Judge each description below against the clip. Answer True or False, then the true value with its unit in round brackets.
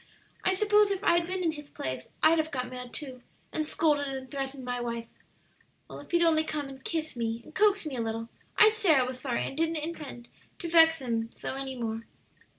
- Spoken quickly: True (220 wpm)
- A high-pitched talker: True (285 Hz)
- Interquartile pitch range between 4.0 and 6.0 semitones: True (4.7 semitones)